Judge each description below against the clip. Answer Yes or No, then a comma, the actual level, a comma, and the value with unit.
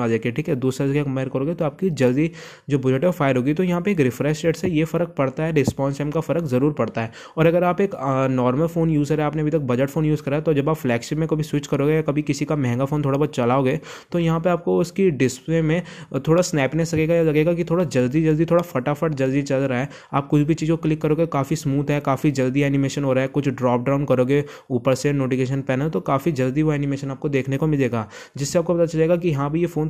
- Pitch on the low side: No, medium, 145 Hz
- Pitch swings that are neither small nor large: Yes, average, 3.3 semitones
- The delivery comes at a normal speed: No, fast, 225 wpm